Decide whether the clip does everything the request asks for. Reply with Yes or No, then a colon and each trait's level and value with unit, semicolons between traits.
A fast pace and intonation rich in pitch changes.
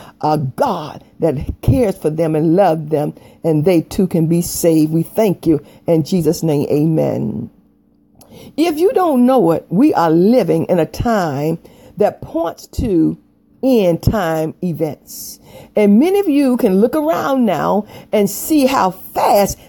No: average, 155 wpm; wide, 6.8 semitones